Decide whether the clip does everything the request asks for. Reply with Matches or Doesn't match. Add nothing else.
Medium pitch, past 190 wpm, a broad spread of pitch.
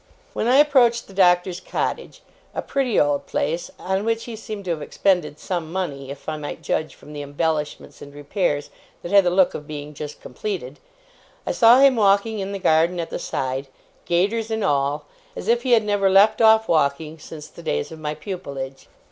Matches